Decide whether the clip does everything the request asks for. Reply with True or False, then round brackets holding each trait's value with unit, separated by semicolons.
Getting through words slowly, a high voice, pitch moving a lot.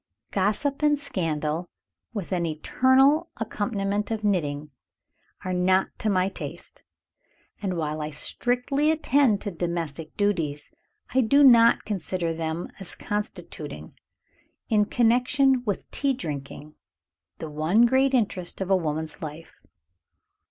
True (125 wpm; 195 Hz; 6.9 semitones)